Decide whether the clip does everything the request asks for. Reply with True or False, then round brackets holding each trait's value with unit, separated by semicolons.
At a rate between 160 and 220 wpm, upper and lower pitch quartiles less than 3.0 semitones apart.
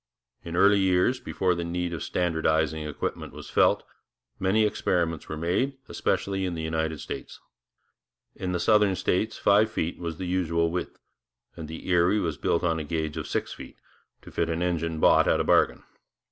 True (180 wpm; 2.5 semitones)